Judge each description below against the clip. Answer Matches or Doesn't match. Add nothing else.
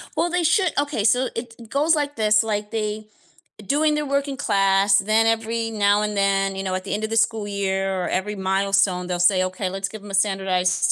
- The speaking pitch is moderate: Doesn't match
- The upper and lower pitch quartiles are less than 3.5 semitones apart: Matches